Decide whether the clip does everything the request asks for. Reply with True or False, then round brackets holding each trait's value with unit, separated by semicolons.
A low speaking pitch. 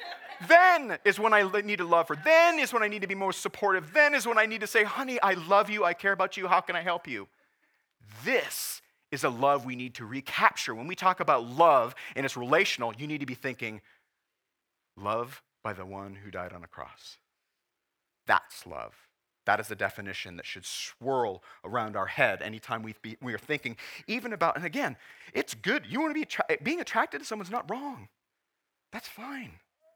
False (180 Hz)